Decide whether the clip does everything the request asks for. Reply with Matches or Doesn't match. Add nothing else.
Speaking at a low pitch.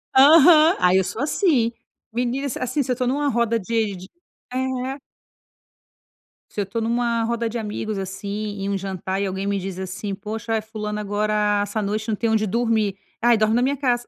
Doesn't match